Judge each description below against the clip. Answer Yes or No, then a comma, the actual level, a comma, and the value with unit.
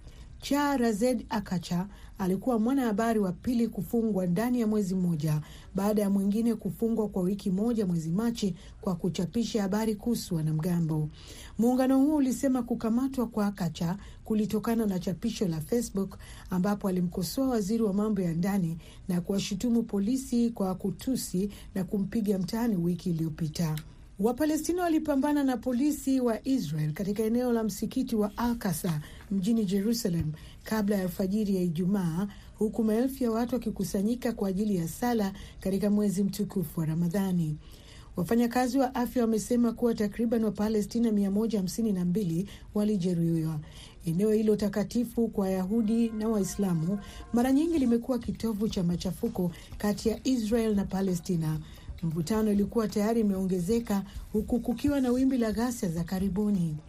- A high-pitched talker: Yes, high, 210 Hz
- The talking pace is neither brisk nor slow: Yes, average, 130 wpm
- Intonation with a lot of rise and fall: No, average, 3.7 semitones